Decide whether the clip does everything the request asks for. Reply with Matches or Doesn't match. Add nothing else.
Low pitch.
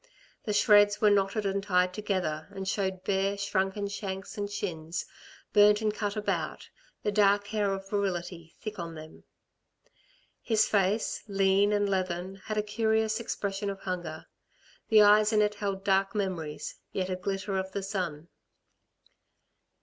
Doesn't match